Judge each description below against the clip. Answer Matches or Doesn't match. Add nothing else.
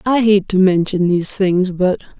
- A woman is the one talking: Matches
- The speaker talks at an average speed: Matches